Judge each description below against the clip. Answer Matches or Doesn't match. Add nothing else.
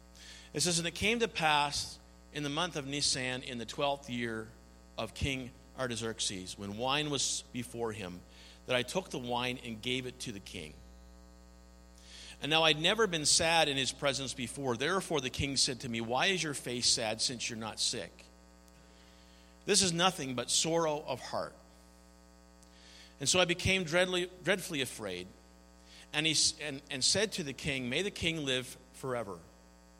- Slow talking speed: Doesn't match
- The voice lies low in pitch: Matches